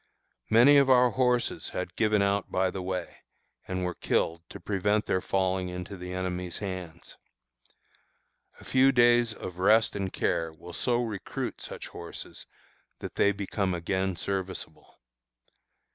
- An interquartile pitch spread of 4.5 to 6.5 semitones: No, average, 3.3 semitones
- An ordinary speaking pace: Yes, average, 145 wpm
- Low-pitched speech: Yes, very low, 95 Hz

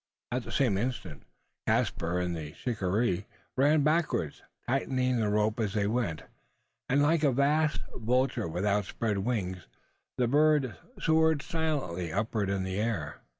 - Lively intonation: Yes, wide, 6.3 semitones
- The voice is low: Yes, low, 115 Hz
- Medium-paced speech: Yes, average, 145 wpm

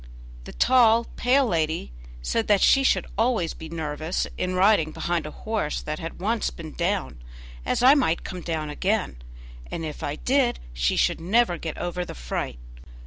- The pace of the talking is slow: No, average, 175 wpm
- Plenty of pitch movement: Yes, wide, 6.2 semitones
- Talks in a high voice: No, medium, 175 Hz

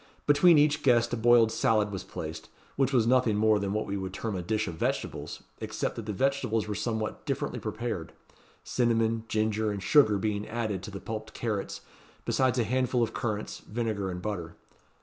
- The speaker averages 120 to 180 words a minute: No, average, 190 wpm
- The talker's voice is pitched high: No, low, 110 Hz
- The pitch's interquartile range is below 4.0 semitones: Yes, average, 2.7 semitones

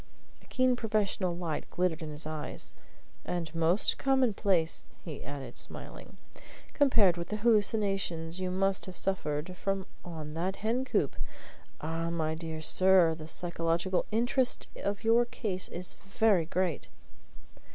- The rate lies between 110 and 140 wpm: Yes, slow, 135 wpm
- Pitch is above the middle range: No, medium, 180 Hz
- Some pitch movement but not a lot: Yes, average, 4.1 semitones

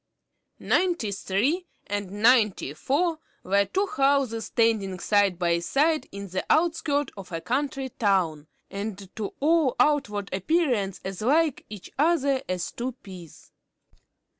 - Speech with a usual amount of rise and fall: No, wide, 6.8 semitones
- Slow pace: Yes, slow, 130 wpm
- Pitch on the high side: Yes, high, 225 Hz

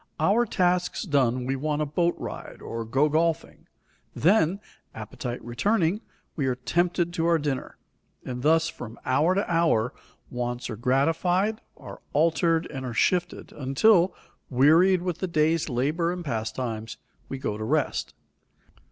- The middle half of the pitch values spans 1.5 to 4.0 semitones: No, wide, 5.5 semitones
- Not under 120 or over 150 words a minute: Yes, average, 145 wpm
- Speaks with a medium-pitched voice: Yes, medium, 155 Hz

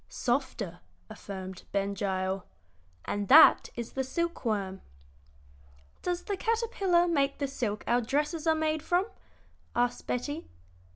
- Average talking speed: No, slow, 125 wpm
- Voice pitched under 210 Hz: No, very high, 265 Hz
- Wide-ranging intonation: Yes, wide, 8.0 semitones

